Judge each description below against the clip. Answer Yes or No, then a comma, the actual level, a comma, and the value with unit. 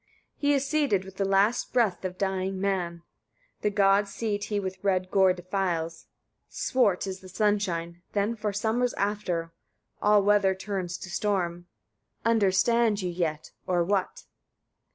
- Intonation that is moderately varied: No, narrow, 2.2 semitones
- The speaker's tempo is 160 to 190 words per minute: No, average, 150 wpm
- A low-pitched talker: No, high, 195 Hz